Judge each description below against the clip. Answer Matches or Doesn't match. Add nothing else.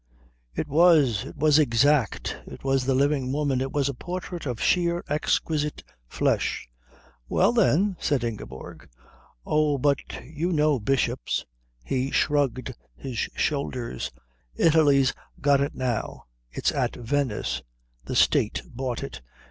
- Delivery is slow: Matches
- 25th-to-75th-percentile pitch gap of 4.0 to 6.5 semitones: Doesn't match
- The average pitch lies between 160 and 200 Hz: Doesn't match